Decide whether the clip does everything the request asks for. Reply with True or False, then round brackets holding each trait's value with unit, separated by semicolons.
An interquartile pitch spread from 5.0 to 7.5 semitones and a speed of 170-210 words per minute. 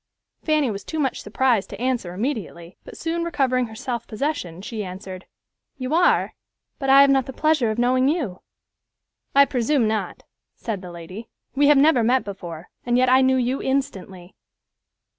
True (5.4 semitones; 175 wpm)